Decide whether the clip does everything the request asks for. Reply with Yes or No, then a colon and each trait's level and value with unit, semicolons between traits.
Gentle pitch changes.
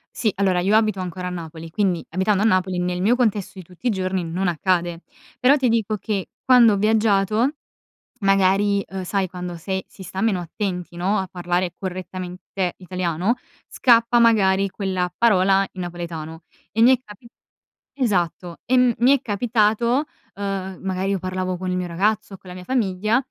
No: average, 3.0 semitones